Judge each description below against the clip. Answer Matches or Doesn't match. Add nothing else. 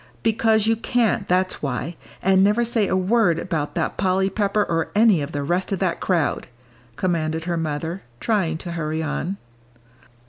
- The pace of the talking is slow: Doesn't match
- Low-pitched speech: Doesn't match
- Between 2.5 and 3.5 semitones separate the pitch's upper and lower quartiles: Doesn't match